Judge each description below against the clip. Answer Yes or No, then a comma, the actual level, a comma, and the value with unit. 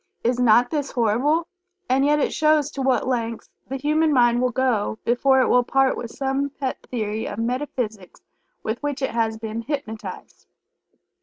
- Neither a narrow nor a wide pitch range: Yes, average, 3.3 semitones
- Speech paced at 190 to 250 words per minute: No, average, 170 wpm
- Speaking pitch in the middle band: No, very high, 255 Hz